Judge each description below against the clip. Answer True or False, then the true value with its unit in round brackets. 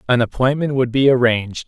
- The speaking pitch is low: True (125 Hz)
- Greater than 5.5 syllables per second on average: True (6.0 syllables/s)